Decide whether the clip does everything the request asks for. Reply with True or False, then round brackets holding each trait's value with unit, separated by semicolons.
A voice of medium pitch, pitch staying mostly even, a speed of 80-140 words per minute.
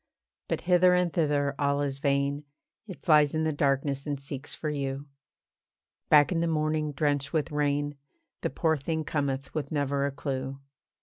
False (145 Hz; 1.9 semitones; 170 wpm)